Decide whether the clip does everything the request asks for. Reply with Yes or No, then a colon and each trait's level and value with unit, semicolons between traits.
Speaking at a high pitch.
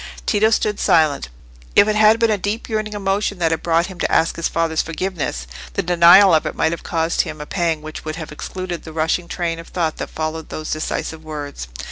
No: medium, 165 Hz